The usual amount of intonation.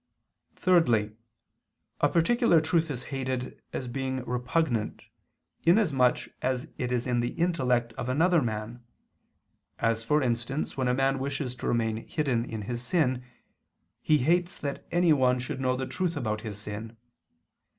Yes: average, 4.2 semitones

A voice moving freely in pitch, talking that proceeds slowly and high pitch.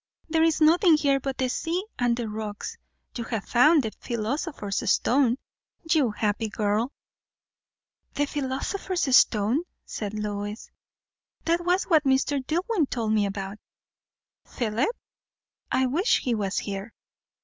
Yes: wide, 6.5 semitones; slow, 130 wpm; very high, 255 Hz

